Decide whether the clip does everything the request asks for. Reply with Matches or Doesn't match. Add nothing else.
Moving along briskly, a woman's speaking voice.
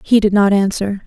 Matches